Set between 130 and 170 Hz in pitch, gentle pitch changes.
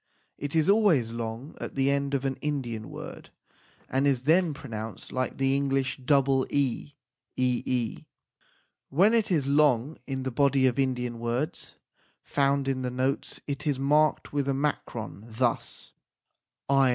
Yes: low, 135 Hz; narrow, 2.1 semitones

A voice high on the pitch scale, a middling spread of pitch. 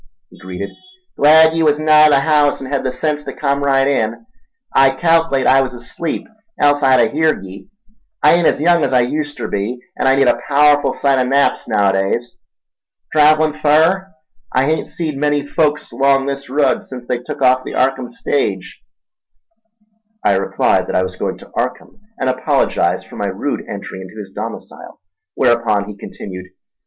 No: medium, 140 Hz; average, 3.6 semitones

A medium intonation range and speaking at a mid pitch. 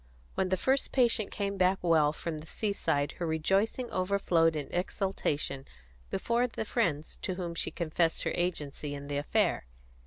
Yes: average, 4.6 semitones; medium, 175 Hz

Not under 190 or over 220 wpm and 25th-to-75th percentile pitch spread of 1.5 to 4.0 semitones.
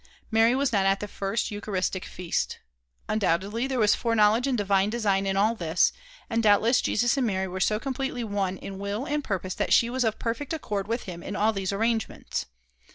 Yes: average, 200 wpm; average, 3.2 semitones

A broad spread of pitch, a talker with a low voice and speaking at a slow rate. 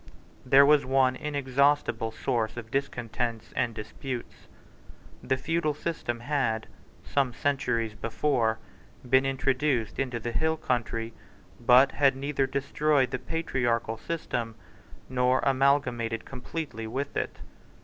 No: average, 3.2 semitones; low, 130 Hz; slow, 115 wpm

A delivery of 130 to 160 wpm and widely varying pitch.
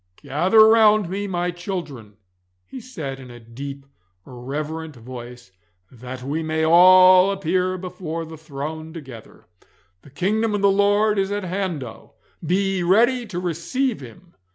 Yes: average, 150 wpm; wide, 5.9 semitones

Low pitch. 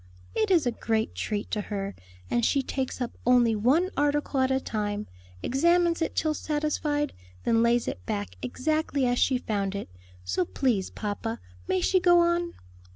No: very high, 250 Hz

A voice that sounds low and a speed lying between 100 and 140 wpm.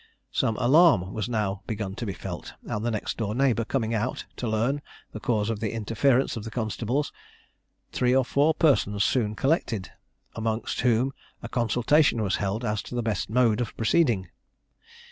No: low, 115 Hz; average, 175 wpm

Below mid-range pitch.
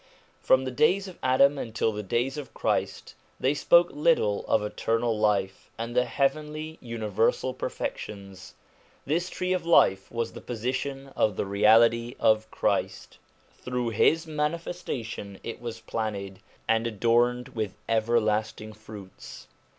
Yes: low, 115 Hz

